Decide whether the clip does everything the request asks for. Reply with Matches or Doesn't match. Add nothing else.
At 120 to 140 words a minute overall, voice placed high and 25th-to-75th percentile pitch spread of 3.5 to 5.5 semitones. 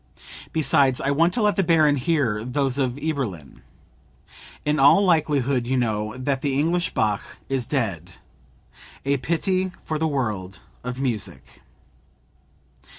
Doesn't match